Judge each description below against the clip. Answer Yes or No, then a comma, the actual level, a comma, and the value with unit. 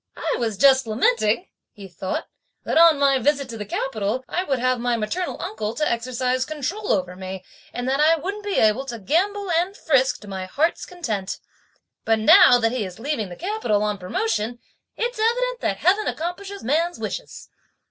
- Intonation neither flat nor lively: No, wide, 8.0 semitones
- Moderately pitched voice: No, very high, 255 Hz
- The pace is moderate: Yes, average, 185 wpm